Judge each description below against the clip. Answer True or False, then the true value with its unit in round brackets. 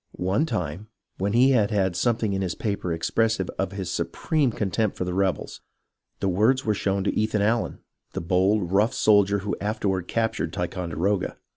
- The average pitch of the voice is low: True (100 Hz)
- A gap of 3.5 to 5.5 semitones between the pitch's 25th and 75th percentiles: False (2.9 semitones)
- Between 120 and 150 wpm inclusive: False (175 wpm)